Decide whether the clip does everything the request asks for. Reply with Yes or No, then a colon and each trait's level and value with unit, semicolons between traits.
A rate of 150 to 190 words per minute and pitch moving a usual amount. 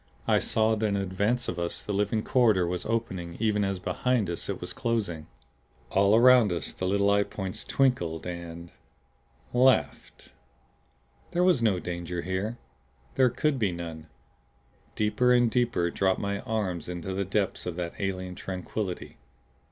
Yes: average, 155 wpm; average, 4.1 semitones